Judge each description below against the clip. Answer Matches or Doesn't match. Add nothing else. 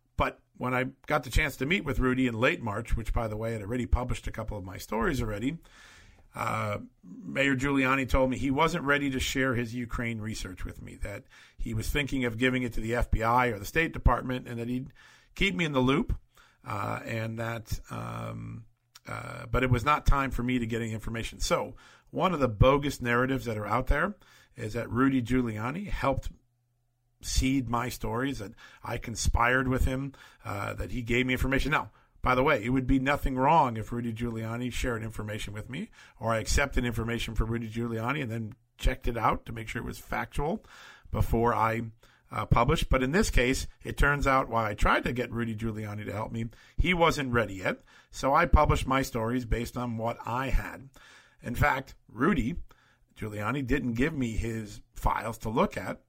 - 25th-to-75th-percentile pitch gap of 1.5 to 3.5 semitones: Matches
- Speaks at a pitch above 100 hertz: Matches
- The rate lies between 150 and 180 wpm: Doesn't match